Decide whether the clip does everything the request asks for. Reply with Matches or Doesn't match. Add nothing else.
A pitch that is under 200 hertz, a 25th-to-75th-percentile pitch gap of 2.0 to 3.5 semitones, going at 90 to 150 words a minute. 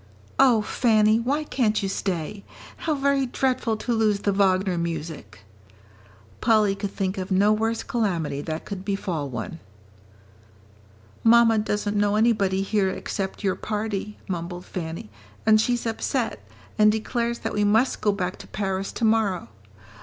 Doesn't match